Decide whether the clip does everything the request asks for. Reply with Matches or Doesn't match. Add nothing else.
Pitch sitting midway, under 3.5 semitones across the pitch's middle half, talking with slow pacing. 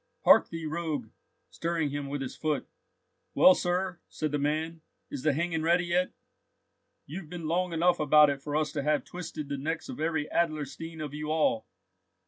Doesn't match